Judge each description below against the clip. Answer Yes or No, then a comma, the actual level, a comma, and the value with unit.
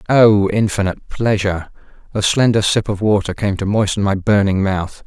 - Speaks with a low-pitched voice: Yes, low, 100 Hz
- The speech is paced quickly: No, average, 165 wpm